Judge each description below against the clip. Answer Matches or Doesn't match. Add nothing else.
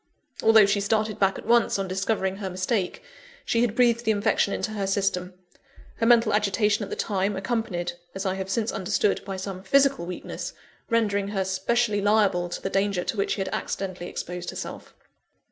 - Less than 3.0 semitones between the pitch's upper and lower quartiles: Matches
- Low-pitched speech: Doesn't match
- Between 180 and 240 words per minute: Matches